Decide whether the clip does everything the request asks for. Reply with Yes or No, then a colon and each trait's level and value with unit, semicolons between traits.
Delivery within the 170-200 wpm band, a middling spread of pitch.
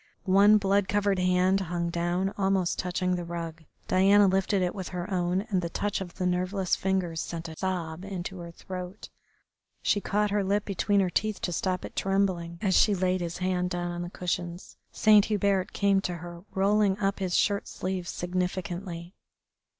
No: average, 180 wpm; narrow, 2.0 semitones